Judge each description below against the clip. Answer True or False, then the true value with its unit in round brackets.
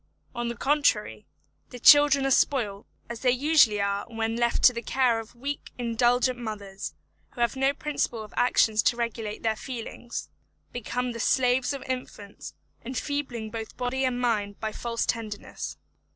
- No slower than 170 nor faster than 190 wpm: False (160 wpm)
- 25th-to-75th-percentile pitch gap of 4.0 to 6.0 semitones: False (2.6 semitones)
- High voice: True (240 Hz)